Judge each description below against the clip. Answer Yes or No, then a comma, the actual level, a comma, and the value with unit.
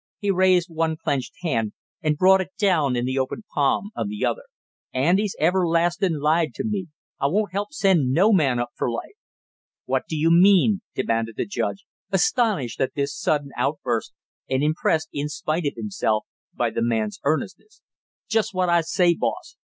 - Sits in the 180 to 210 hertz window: No, medium, 160 Hz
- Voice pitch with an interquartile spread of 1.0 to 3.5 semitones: No, wide, 5.6 semitones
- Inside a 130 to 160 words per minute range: No, average, 175 wpm